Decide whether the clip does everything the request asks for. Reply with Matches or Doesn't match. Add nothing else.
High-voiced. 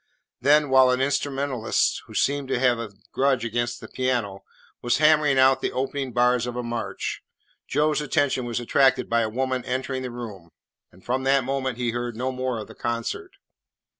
Doesn't match